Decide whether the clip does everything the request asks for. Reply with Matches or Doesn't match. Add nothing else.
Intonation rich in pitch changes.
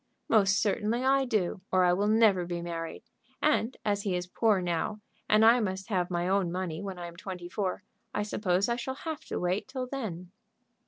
Doesn't match